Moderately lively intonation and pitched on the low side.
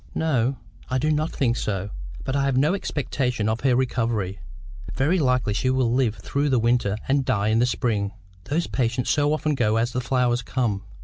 Yes: average, 3.3 semitones; low, 125 Hz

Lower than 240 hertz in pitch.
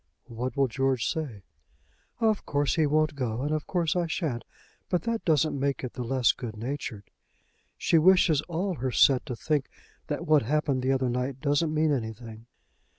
Yes: medium, 140 Hz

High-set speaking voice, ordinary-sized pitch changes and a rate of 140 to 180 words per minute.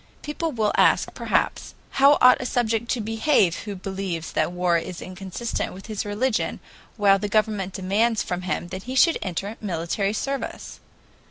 Yes: high, 205 Hz; average, 4.0 semitones; average, 165 wpm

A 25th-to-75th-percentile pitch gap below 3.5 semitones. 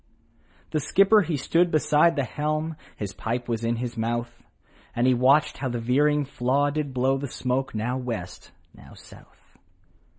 No: average, 4.0 semitones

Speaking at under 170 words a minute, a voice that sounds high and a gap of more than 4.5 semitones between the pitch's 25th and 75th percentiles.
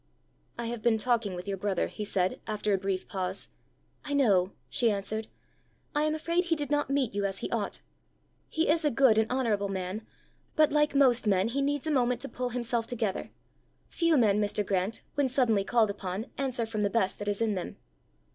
No: fast, 205 wpm; high, 225 Hz; average, 5.0 semitones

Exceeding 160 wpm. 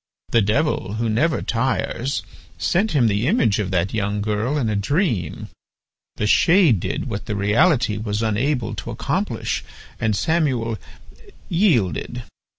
No: average, 140 wpm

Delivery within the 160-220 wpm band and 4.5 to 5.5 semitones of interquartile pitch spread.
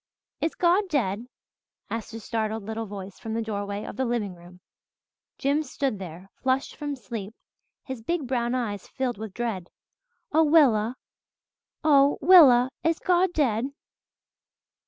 No: average, 140 wpm; average, 5.1 semitones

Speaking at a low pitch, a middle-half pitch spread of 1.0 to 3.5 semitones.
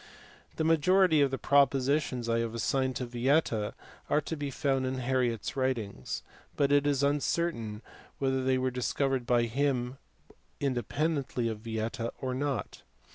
Yes: low, 130 Hz; average, 3.1 semitones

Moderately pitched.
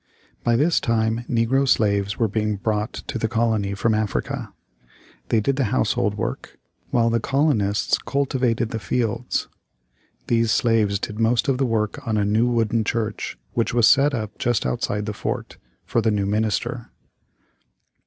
No: low, 115 Hz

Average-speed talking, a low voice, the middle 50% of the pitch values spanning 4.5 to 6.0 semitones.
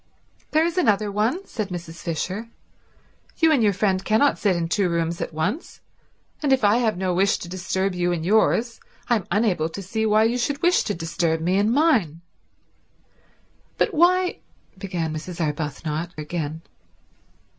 No: average, 165 wpm; high, 195 Hz; average, 5.2 semitones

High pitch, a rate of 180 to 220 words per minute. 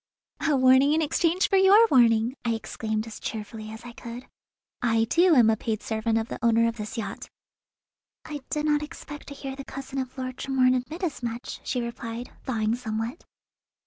Yes: high, 245 Hz; average, 190 wpm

